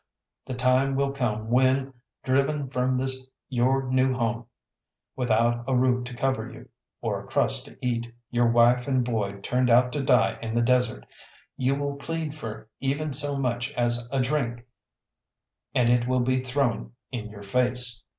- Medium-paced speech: Yes, average, 170 wpm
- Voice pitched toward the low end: Yes, low, 125 Hz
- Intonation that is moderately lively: No, narrow, 1.9 semitones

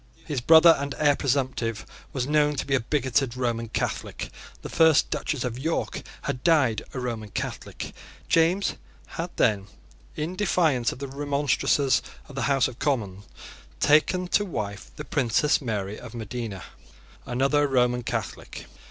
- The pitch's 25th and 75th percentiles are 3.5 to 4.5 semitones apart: Yes, average, 4.0 semitones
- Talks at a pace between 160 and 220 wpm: No, average, 150 wpm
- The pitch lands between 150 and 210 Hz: No, low, 135 Hz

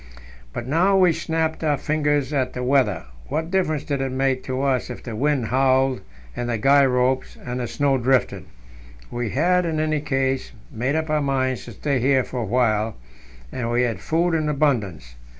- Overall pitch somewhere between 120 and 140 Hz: Yes, low, 135 Hz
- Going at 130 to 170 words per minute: No, average, 190 wpm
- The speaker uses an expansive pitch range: No, average, 3.4 semitones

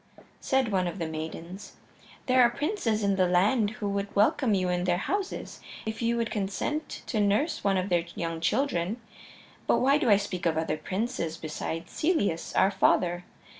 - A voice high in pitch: Yes, high, 200 Hz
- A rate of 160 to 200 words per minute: Yes, average, 180 wpm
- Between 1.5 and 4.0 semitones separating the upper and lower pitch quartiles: No, average, 5.1 semitones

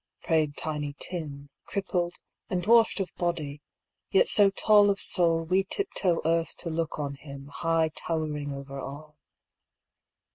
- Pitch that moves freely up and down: No, average, 3.8 semitones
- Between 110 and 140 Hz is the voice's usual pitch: No, medium, 165 Hz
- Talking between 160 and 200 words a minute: No, average, 145 wpm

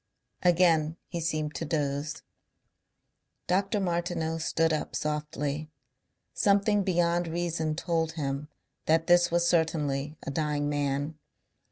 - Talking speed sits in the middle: No, slow, 115 wpm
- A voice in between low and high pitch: Yes, medium, 160 Hz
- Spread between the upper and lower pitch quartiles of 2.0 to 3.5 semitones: Yes, narrow, 2.4 semitones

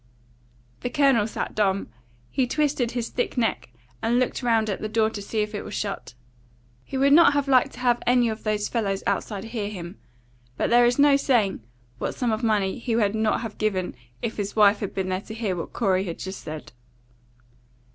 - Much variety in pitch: No, average, 3.4 semitones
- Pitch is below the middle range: No, high, 220 Hz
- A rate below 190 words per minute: No, fast, 205 wpm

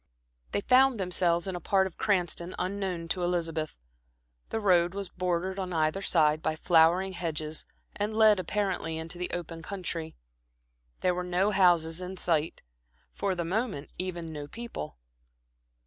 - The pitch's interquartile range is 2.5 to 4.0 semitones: Yes, average, 2.8 semitones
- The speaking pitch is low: No, medium, 180 Hz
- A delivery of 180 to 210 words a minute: No, average, 150 wpm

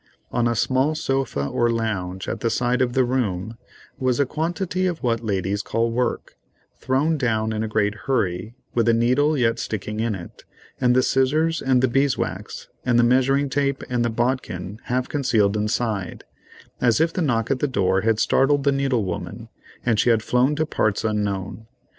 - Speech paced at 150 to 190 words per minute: Yes, average, 185 wpm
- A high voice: No, low, 120 Hz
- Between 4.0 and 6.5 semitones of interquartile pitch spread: No, average, 3.6 semitones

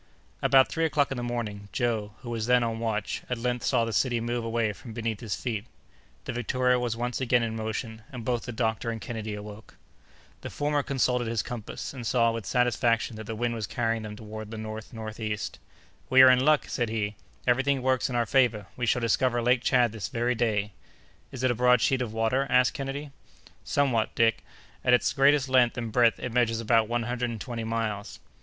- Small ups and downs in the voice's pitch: Yes, narrow, 2.0 semitones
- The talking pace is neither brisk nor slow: No, fast, 215 wpm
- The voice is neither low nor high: No, low, 120 Hz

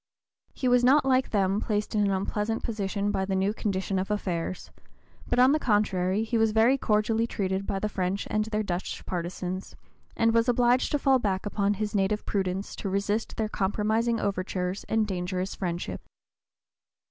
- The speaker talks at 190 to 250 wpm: No, average, 175 wpm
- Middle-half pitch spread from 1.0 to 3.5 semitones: Yes, average, 2.7 semitones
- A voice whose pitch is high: Yes, high, 205 Hz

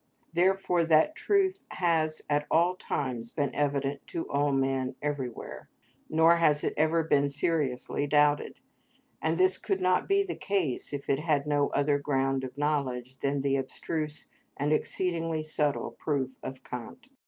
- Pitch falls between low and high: Yes, medium, 150 Hz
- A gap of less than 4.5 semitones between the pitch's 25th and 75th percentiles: Yes, average, 3.2 semitones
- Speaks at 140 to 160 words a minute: Yes, average, 155 wpm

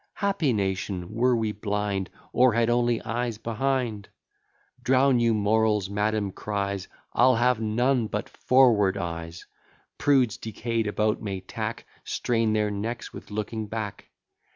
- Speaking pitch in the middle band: No, low, 110 Hz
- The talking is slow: Yes, slow, 130 wpm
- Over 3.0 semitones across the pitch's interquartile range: No, average, 2.7 semitones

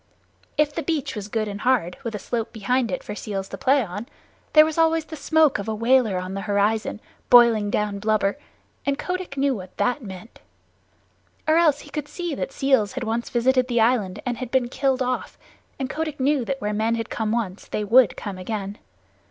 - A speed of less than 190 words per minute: No, fast, 205 wpm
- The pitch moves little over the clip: No, average, 4.6 semitones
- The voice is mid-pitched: No, high, 235 Hz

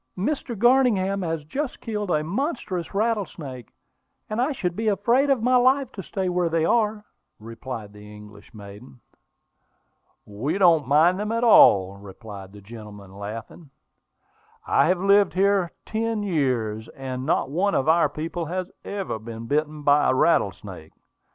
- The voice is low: No, medium, 165 Hz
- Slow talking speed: No, average, 155 wpm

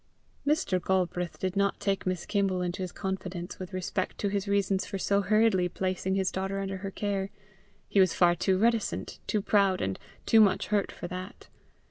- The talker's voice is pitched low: No, high, 190 Hz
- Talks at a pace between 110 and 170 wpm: No, average, 185 wpm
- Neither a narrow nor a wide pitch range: No, narrow, 1.4 semitones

